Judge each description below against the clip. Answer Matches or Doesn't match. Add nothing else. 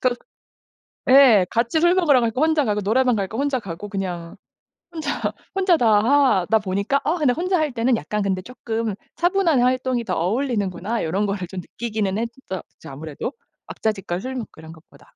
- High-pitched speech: Matches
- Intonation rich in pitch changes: Matches